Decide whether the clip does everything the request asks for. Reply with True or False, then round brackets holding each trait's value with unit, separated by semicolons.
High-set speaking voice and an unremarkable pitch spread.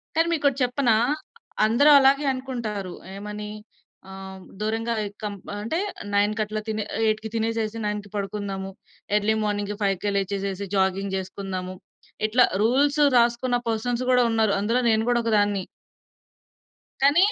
True (215 Hz; 3.2 semitones)